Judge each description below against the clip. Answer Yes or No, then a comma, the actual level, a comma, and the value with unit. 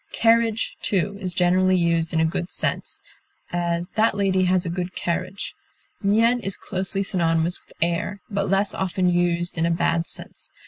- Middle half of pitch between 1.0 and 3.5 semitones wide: Yes, narrow, 2.4 semitones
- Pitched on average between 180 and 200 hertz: Yes, medium, 185 Hz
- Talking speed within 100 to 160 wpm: No, average, 170 wpm